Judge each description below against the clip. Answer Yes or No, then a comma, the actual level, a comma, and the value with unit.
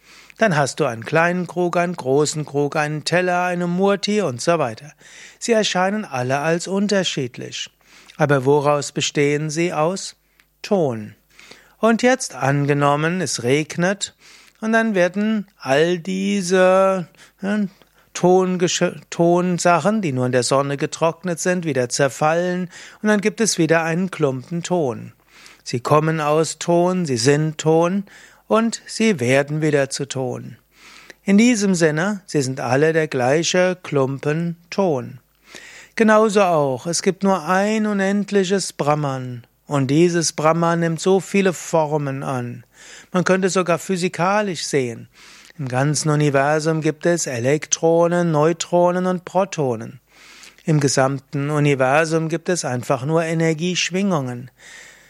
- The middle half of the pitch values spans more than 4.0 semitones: Yes, average, 4.4 semitones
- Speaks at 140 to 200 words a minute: No, average, 130 wpm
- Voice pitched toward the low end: No, medium, 165 Hz